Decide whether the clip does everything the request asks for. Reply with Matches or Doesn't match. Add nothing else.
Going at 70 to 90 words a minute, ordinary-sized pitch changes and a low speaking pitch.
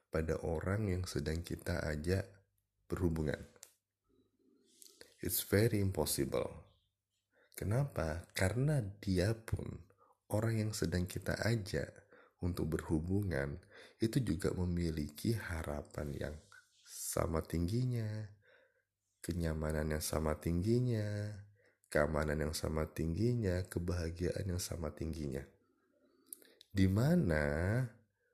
Matches